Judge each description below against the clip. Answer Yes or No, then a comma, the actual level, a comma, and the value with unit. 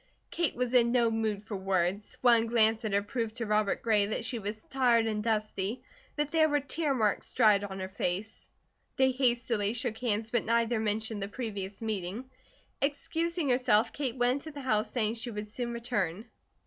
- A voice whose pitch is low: No, high, 225 Hz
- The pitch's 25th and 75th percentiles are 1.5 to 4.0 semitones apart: Yes, average, 3.1 semitones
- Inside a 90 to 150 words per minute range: No, average, 185 wpm